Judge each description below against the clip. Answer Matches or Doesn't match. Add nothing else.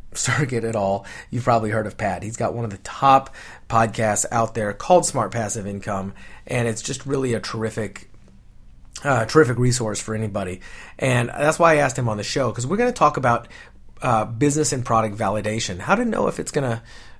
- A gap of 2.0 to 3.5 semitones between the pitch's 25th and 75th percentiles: Doesn't match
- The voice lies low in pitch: Matches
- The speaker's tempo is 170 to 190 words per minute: Doesn't match